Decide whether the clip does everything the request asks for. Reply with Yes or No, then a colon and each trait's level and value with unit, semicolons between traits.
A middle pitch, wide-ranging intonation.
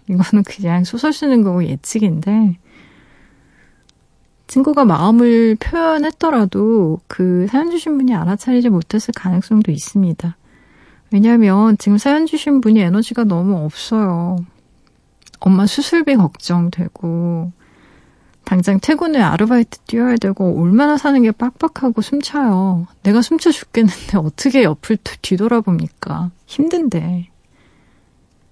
No: high, 215 Hz; wide, 5.8 semitones